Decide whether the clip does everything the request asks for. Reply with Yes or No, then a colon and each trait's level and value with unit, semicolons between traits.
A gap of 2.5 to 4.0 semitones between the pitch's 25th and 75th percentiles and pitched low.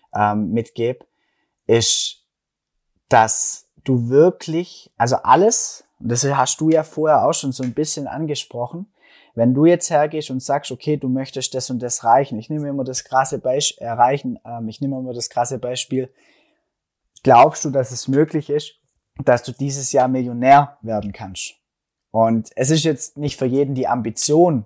Yes: average, 3.5 semitones; low, 130 Hz